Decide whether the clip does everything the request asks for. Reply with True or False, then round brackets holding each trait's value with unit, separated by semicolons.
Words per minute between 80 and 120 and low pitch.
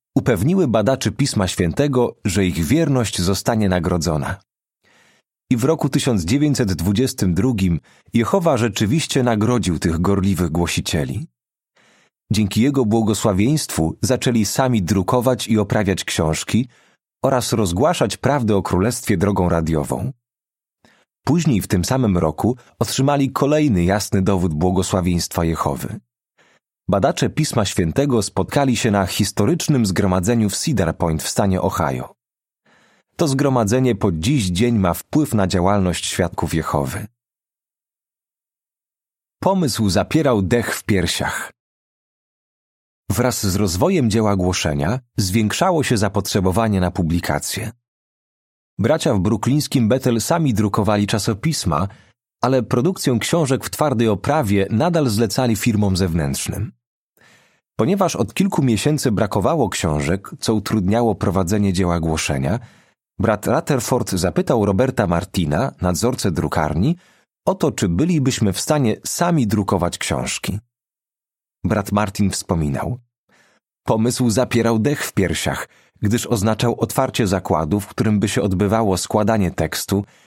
True (110 wpm; 110 Hz)